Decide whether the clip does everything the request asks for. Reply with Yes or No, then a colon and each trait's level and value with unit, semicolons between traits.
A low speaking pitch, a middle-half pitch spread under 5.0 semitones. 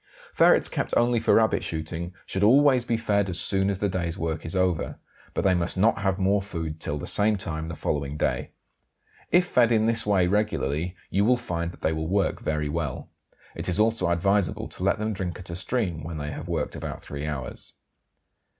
Yes: very low, 95 Hz; average, 4.4 semitones